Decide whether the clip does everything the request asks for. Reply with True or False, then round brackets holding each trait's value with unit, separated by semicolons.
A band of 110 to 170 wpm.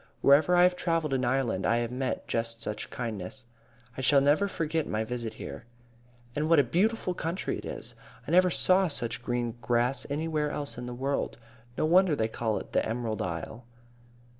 False (190 wpm)